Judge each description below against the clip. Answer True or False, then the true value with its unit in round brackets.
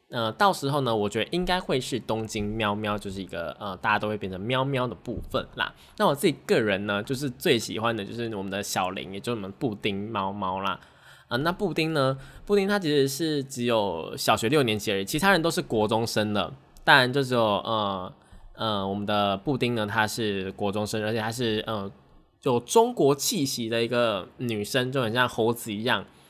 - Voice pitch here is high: False (110 Hz)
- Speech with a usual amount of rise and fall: True (4.4 semitones)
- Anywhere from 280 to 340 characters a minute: True (305 characters per minute)